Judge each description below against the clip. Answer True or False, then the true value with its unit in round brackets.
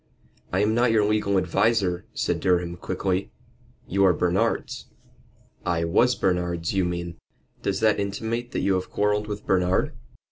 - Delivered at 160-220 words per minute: False (150 wpm)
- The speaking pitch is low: True (95 Hz)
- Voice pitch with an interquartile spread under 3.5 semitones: True (2.9 semitones)